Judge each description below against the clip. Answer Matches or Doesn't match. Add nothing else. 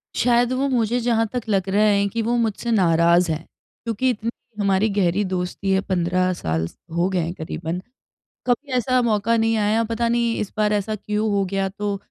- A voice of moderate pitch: Doesn't match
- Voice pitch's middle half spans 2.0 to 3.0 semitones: Doesn't match